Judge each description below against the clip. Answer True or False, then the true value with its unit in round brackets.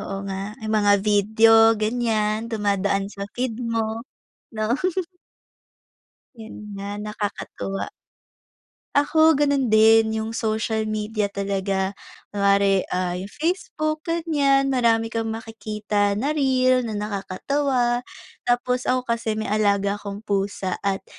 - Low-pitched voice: False (220 Hz)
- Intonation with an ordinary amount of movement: True (3.2 semitones)